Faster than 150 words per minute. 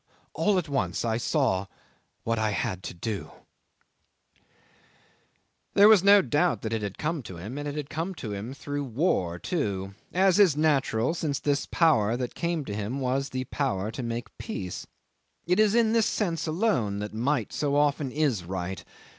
Yes: average, 175 wpm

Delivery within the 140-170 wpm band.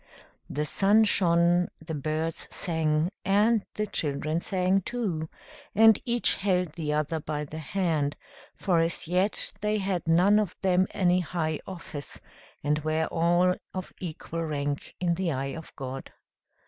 Yes: average, 150 wpm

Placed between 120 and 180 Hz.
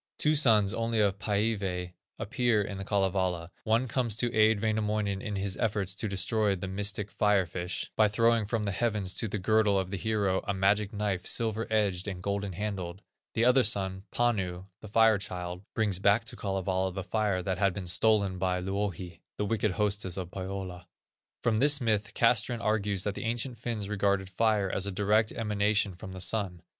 No: low, 100 Hz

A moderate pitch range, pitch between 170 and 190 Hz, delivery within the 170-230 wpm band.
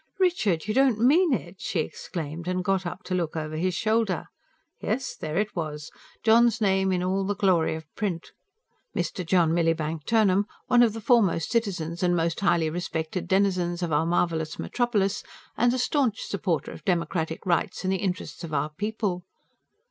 Yes: average, 4.4 semitones; medium, 185 Hz; average, 175 wpm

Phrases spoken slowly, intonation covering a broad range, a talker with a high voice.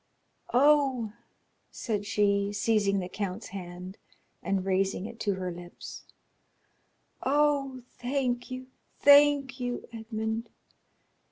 No: slow, 100 wpm; average, 4.7 semitones; high, 220 Hz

